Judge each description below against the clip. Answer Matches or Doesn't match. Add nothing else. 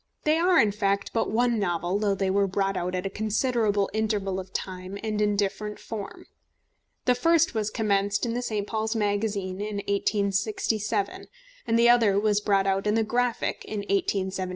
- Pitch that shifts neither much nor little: Doesn't match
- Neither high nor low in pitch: Doesn't match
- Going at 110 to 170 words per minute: Doesn't match